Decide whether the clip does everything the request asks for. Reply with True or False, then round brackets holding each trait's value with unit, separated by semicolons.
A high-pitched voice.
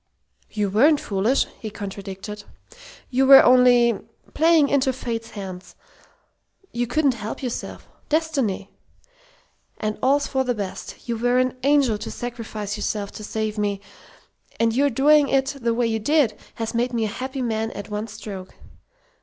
True (235 Hz)